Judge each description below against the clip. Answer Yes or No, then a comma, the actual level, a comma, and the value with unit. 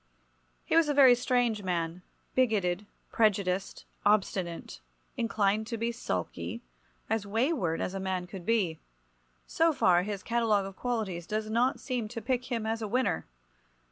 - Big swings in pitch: No, average, 4.1 semitones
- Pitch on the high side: Yes, high, 215 Hz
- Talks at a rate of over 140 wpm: Yes, average, 150 wpm